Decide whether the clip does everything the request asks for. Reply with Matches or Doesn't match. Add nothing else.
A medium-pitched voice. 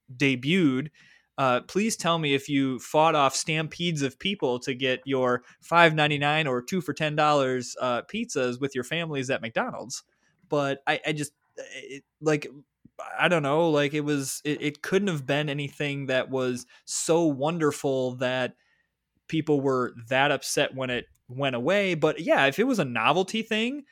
Matches